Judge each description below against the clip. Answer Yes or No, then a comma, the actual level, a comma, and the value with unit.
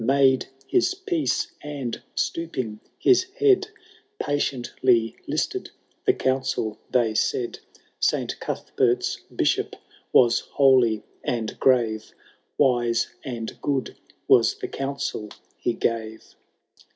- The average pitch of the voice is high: No, low, 130 Hz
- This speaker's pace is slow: Yes, slow, 100 wpm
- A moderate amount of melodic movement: Yes, average, 3.3 semitones